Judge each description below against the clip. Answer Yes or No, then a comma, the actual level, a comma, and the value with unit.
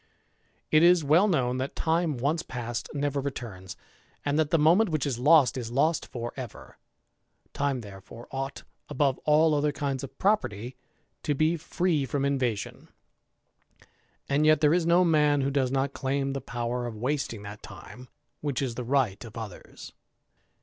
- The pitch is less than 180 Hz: Yes, medium, 140 Hz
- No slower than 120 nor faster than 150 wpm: No, average, 170 wpm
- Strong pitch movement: No, average, 3.8 semitones